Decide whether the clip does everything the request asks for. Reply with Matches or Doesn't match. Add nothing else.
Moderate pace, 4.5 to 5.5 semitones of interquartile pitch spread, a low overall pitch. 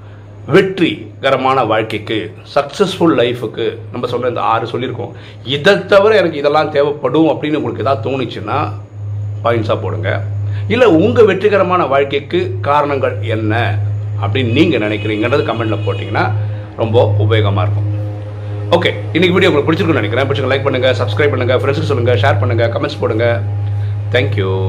Matches